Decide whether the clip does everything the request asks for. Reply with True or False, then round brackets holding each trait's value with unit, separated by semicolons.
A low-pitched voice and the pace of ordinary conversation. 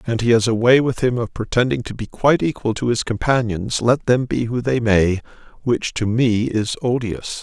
False (115 Hz; 220 wpm)